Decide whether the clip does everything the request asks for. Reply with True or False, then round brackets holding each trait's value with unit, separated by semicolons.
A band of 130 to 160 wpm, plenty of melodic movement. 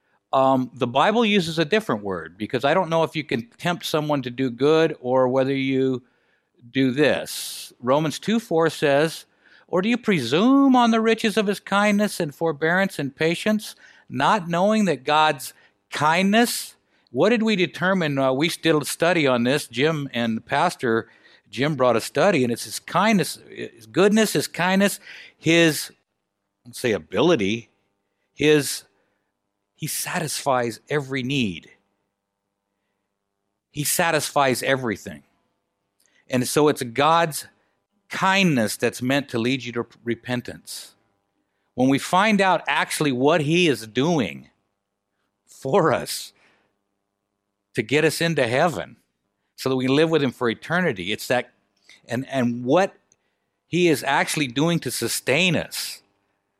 True (145 wpm; 7.2 semitones)